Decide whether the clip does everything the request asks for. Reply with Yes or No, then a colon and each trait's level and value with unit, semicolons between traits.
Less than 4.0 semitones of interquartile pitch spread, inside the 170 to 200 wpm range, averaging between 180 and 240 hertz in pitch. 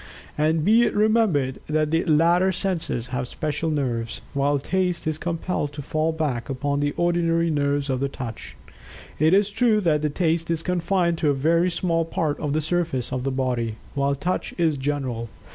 No: average, 3.5 semitones; average, 180 wpm; medium, 155 Hz